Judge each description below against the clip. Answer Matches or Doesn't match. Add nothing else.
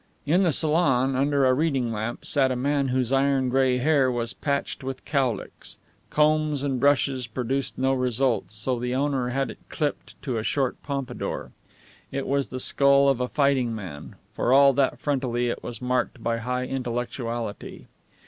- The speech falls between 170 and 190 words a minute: Matches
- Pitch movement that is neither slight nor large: Doesn't match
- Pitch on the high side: Doesn't match